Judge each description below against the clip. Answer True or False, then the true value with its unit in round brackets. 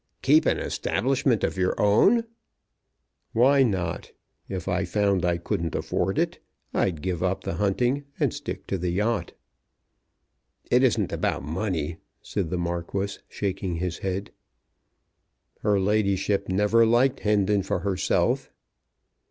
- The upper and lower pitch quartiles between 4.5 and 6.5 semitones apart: False (2.9 semitones)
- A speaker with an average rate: False (130 wpm)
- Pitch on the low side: True (95 Hz)